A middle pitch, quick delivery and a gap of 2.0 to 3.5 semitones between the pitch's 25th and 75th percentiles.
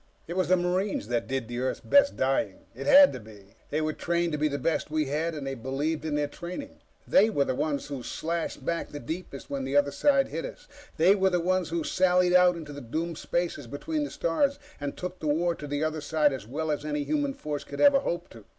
No: medium, 155 Hz; fast, 240 wpm; average, 4.0 semitones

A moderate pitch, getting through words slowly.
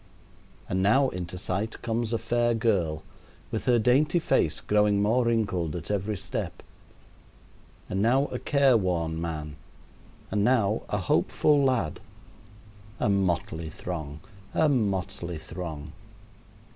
No: low, 100 Hz; slow, 125 wpm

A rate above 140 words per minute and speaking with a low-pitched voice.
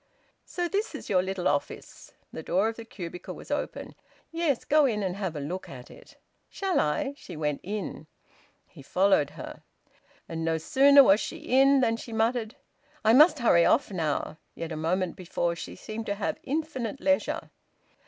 No: average, 180 wpm; high, 205 Hz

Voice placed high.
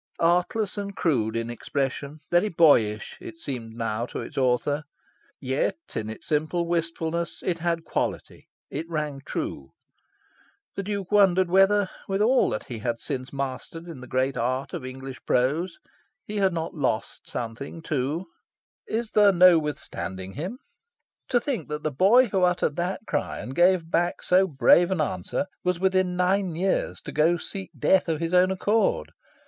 No: medium, 165 Hz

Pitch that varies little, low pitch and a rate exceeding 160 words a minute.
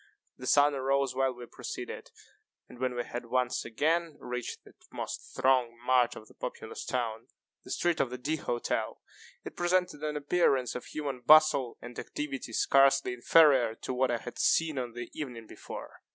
No: average, 3.4 semitones; low, 130 Hz; average, 175 wpm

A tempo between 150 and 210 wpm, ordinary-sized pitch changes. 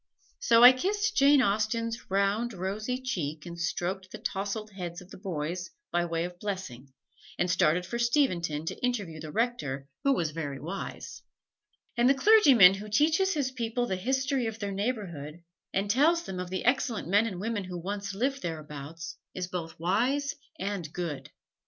No: average, 170 wpm; wide, 5.9 semitones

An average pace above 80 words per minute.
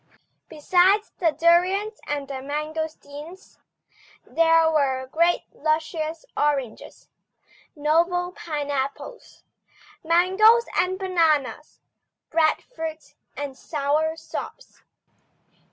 No: slow, 75 wpm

